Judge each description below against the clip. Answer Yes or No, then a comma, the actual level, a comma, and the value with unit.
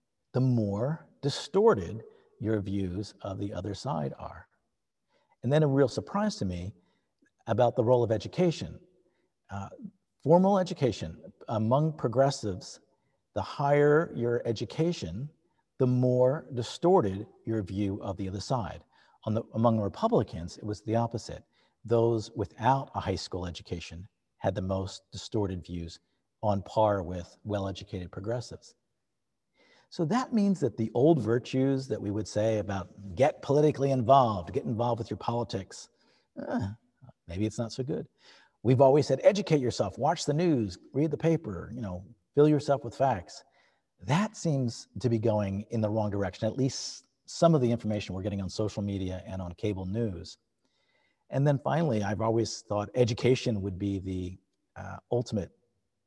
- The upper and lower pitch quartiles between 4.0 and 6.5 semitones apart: Yes, average, 5.2 semitones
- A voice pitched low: Yes, low, 115 Hz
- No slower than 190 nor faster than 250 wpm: No, average, 155 wpm